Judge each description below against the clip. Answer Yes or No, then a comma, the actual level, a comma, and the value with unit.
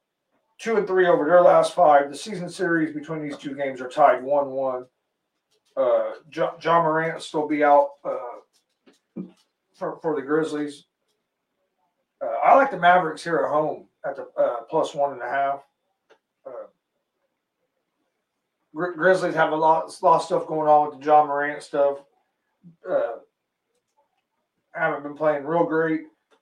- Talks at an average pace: Yes, average, 160 wpm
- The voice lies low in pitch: No, medium, 155 Hz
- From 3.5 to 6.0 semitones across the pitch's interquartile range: No, average, 2.9 semitones